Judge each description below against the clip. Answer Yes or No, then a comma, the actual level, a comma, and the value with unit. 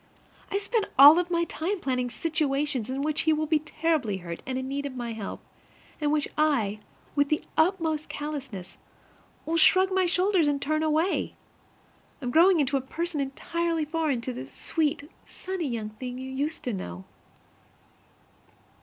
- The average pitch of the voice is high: Yes, very high, 295 Hz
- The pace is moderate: Yes, average, 170 wpm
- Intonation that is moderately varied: Yes, average, 4.0 semitones